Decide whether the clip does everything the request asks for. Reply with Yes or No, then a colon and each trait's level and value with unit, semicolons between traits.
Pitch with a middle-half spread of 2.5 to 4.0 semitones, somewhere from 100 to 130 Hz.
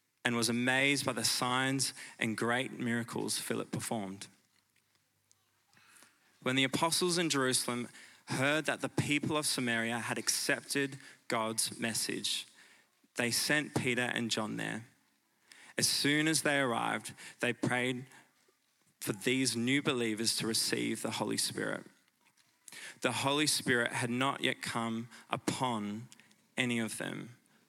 Yes: average, 2.9 semitones; low, 125 Hz